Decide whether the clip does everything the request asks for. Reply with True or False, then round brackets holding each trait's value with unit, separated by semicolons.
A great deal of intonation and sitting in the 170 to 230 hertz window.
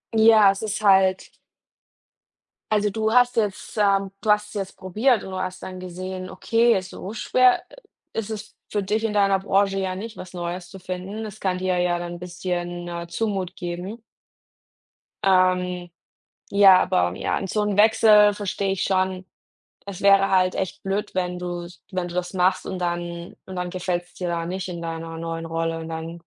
False (2.4 semitones; 185 Hz)